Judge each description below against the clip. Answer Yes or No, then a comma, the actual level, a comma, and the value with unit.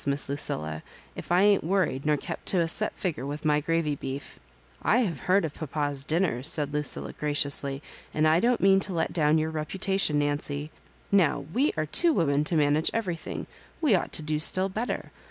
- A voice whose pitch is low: No, medium, 155 Hz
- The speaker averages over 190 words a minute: Yes, average, 200 wpm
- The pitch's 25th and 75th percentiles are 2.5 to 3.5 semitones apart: No, average, 4.3 semitones